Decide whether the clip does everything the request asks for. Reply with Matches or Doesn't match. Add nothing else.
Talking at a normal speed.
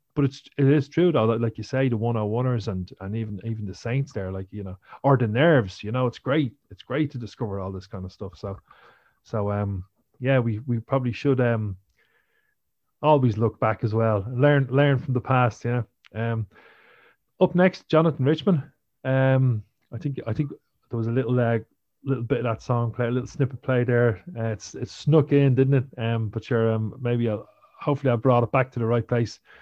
Doesn't match